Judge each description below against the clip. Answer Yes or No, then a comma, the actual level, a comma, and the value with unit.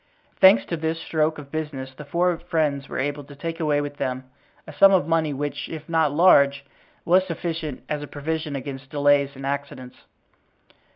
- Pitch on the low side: No, medium, 145 Hz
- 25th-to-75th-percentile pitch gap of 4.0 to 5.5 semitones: No, narrow, 2.5 semitones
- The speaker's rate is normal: Yes, average, 180 wpm